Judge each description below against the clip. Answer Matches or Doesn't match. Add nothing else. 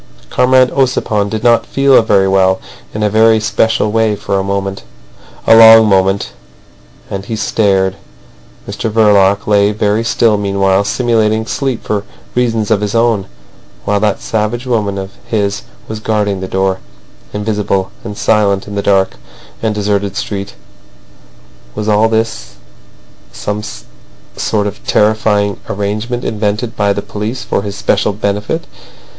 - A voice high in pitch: Doesn't match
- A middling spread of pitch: Doesn't match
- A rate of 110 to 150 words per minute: Matches